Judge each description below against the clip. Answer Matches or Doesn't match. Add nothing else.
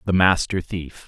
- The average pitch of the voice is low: Matches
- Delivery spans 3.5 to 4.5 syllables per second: Matches